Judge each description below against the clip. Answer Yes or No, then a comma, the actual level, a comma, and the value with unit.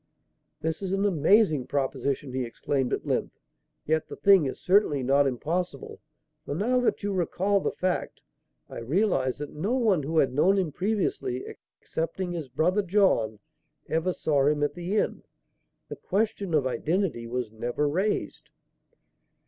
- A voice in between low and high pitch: Yes, medium, 160 Hz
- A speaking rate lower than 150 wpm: No, average, 155 wpm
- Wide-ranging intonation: Yes, wide, 6.1 semitones